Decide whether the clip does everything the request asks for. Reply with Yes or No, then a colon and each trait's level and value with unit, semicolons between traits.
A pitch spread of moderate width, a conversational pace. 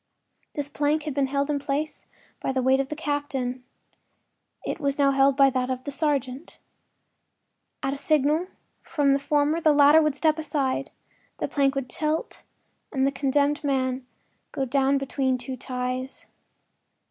No: narrow, 1.8 semitones; average, 160 wpm